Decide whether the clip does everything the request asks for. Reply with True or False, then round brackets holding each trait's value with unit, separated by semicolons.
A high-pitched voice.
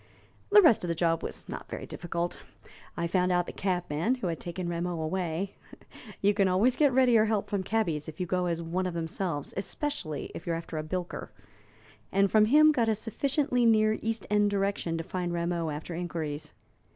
False (180 Hz)